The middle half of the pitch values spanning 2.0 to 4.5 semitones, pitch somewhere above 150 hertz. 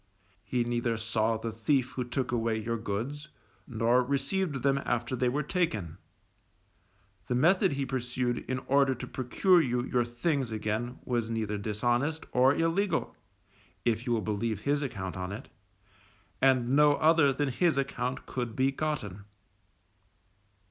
No: average, 3.5 semitones; low, 125 Hz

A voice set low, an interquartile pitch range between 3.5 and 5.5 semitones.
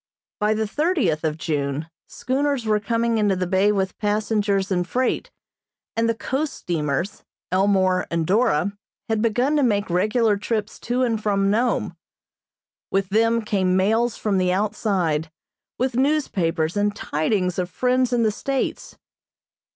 No: high, 210 Hz; average, 4.0 semitones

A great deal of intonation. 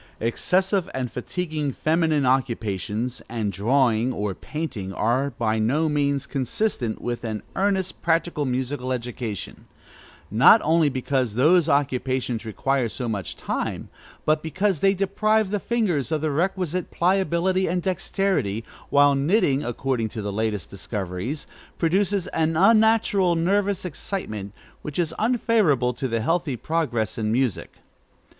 Yes: wide, 7.1 semitones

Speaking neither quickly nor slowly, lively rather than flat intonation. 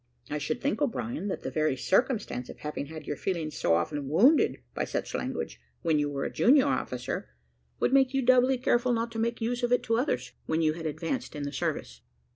No: fast, 220 wpm; wide, 8.8 semitones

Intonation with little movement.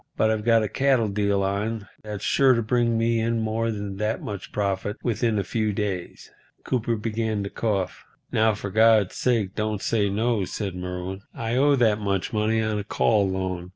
Yes: narrow, 2.3 semitones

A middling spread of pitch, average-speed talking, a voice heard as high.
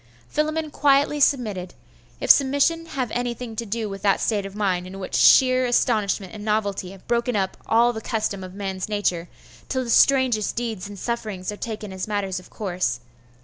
Yes: average, 4.0 semitones; average, 185 wpm; high, 215 Hz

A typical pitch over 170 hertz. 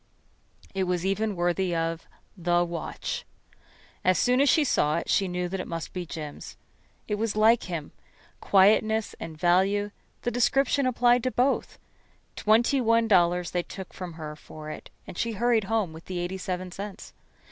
Yes: high, 190 Hz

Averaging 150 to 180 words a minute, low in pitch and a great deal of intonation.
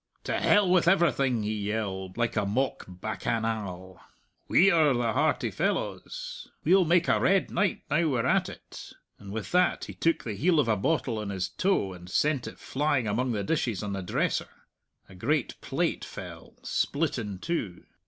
Yes: average, 175 wpm; low, 120 Hz; wide, 8.2 semitones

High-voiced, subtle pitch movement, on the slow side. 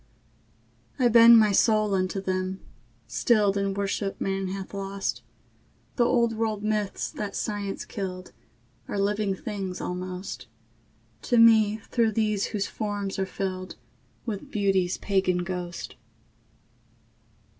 Yes: high, 200 Hz; narrow, 2.0 semitones; slow, 120 wpm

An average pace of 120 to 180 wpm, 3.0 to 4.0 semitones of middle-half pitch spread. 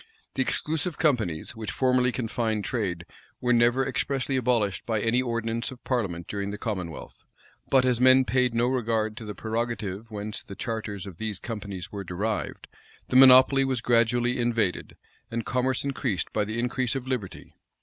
Yes: average, 165 wpm; average, 3.3 semitones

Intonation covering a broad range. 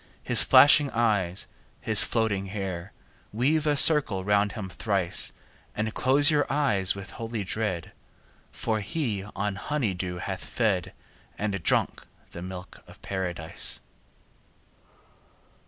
No: average, 4.0 semitones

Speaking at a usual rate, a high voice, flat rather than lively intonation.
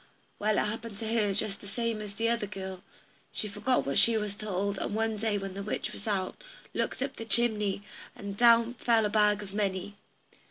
No: fast, 215 wpm; high, 210 Hz; narrow, 2.1 semitones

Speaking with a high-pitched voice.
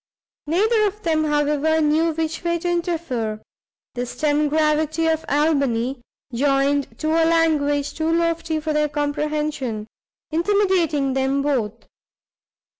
Yes: very high, 305 Hz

